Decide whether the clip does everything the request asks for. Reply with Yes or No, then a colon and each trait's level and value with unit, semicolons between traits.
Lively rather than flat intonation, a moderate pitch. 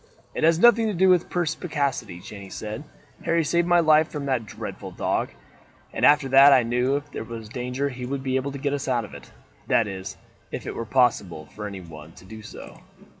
No: wide, 5.7 semitones; low, 130 Hz